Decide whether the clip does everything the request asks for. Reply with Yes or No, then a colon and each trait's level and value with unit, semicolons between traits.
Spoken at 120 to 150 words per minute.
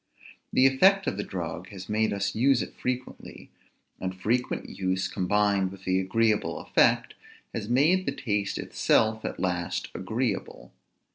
Yes: average, 145 wpm